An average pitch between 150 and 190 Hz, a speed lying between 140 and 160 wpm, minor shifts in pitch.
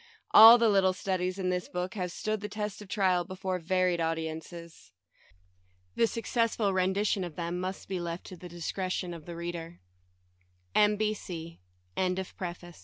Yes: medium, 185 Hz; average, 145 wpm; narrow, 2.1 semitones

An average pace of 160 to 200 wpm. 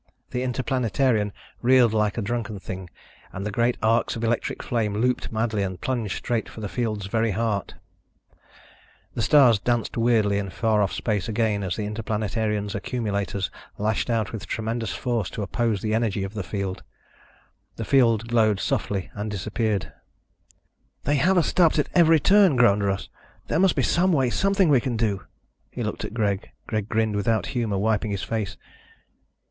Yes: average, 170 wpm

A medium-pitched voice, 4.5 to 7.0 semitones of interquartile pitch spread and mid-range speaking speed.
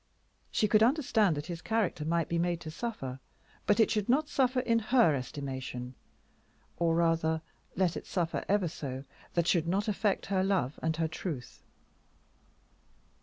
Yes: medium, 170 Hz; average, 5.1 semitones; average, 160 wpm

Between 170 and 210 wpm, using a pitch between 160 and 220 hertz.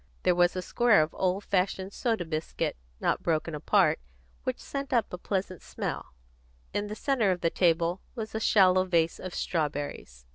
Yes: average, 175 wpm; medium, 185 Hz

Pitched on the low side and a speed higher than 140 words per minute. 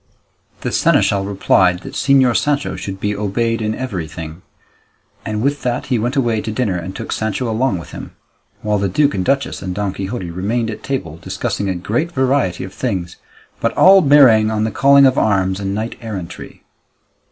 Yes: low, 110 Hz; average, 185 wpm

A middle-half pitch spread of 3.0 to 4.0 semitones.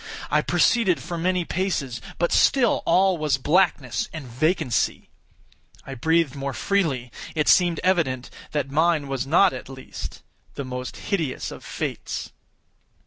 No: average, 5.1 semitones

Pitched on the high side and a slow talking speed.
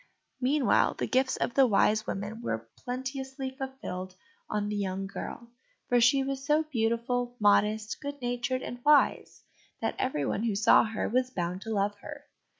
No: high, 240 Hz; average, 160 wpm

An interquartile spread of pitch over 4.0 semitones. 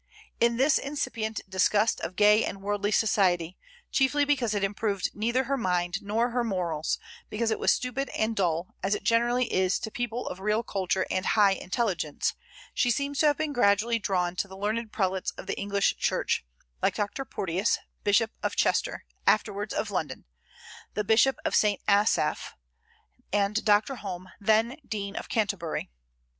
No: average, 3.3 semitones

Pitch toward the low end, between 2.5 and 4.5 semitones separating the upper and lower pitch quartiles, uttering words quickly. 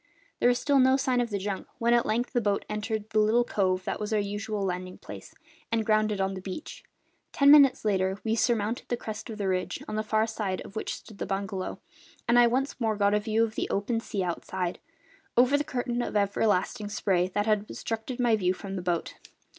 No: high, 215 Hz; average, 3.2 semitones; fast, 225 wpm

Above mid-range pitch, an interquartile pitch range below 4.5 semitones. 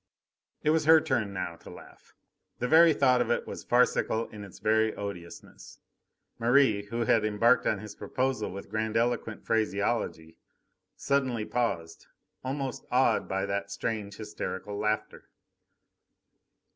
No: low, 110 Hz; average, 3.6 semitones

